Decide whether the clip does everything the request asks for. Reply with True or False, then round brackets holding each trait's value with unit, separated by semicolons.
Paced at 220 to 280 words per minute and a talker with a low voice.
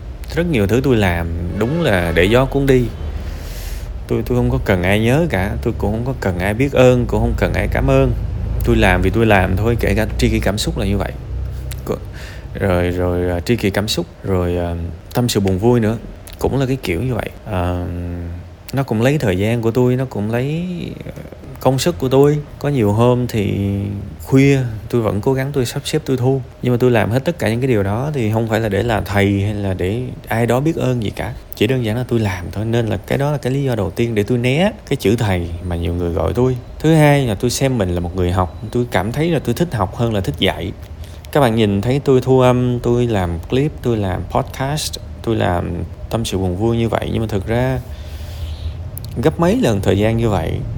True (240 wpm; 110 Hz)